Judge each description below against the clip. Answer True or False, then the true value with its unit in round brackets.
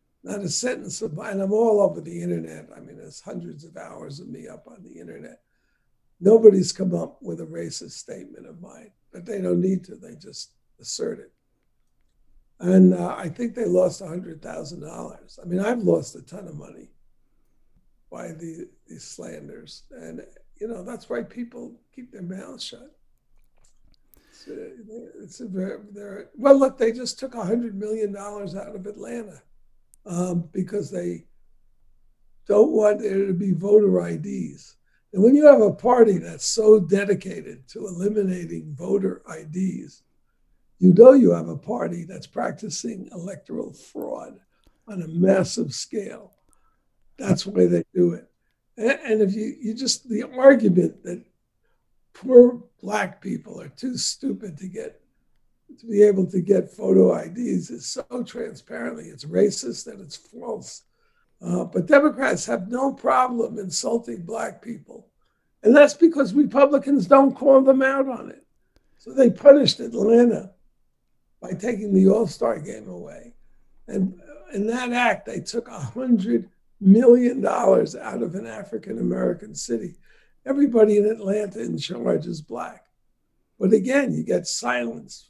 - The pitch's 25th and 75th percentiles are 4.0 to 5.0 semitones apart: True (4.5 semitones)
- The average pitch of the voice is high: True (215 Hz)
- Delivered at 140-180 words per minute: True (150 wpm)